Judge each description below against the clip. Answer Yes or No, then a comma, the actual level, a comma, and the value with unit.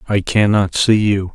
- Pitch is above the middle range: No, low, 100 Hz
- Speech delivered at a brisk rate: No, average, 180 wpm